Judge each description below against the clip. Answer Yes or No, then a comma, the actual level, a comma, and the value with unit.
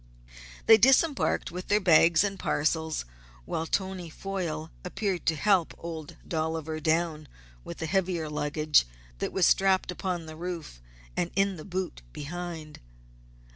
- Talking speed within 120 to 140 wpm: Yes, slow, 135 wpm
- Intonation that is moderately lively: Yes, average, 3.2 semitones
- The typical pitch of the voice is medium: Yes, medium, 170 Hz